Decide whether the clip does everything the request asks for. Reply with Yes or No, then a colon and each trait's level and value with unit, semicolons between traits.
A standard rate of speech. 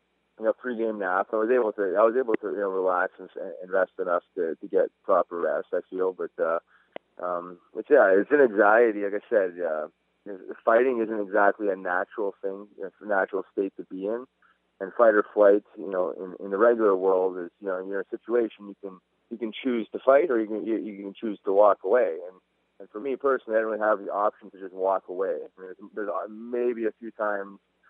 No: fast, 230 wpm